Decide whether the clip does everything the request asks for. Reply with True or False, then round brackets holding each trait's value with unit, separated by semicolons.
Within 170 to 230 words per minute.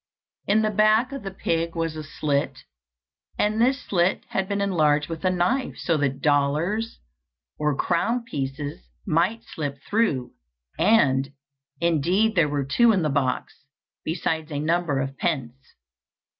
False (145 wpm)